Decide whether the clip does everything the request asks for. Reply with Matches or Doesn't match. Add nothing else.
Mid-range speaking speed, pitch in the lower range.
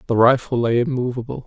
Matches